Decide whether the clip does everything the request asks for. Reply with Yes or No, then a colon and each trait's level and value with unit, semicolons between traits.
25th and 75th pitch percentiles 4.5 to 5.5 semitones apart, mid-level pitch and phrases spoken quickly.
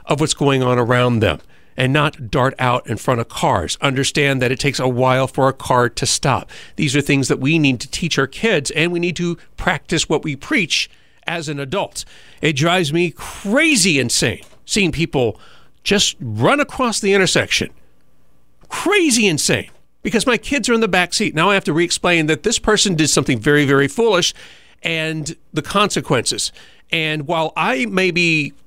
No: average, 5.1 semitones; medium, 155 Hz; average, 185 wpm